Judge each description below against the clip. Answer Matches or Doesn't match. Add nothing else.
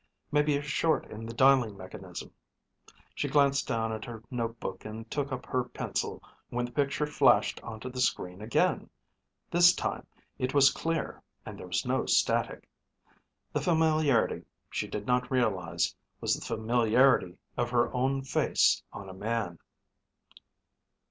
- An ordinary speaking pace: Matches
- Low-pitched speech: Matches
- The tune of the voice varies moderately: Matches